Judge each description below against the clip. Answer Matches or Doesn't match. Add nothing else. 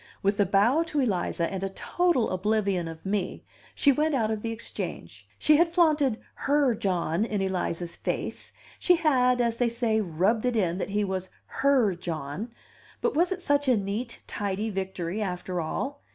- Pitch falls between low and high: Doesn't match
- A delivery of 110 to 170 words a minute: Doesn't match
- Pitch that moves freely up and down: Matches